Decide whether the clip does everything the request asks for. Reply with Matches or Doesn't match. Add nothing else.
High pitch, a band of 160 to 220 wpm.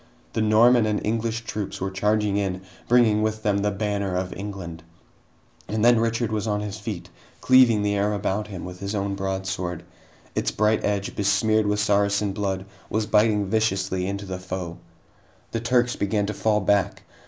Doesn't match